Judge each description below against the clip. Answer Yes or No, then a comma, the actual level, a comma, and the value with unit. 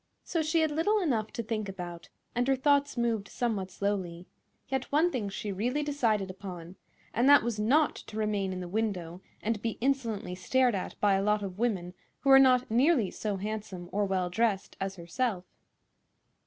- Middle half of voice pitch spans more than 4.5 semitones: Yes, average, 5.1 semitones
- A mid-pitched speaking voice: No, high, 215 Hz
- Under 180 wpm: No, average, 185 wpm